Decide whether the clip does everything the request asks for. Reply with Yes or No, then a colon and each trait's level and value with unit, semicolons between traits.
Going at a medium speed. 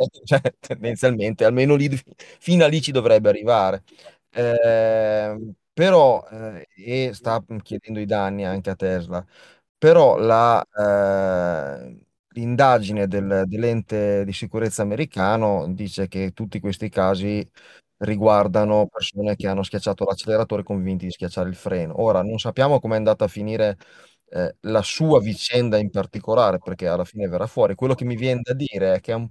Yes: average, 155 wpm